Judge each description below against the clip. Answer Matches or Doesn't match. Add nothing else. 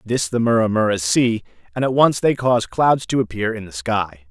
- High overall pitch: Doesn't match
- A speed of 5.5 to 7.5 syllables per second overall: Doesn't match